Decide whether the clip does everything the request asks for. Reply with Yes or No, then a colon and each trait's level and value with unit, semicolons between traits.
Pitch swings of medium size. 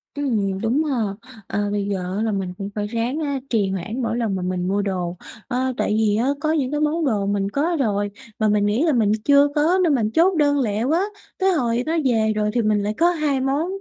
No: wide, 6.0 semitones